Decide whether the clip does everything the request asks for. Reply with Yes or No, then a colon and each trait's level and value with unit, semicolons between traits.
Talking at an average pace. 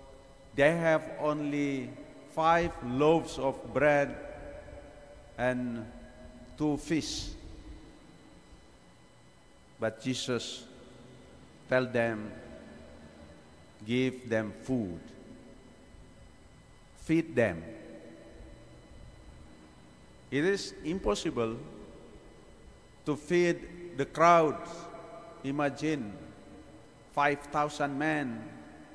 No: slow, 60 wpm